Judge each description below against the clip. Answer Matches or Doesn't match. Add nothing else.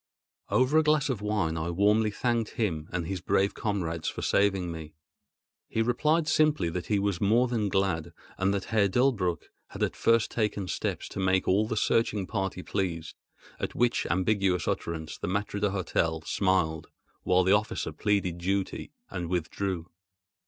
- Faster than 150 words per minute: Matches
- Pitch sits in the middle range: Doesn't match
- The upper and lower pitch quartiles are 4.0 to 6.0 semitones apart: Doesn't match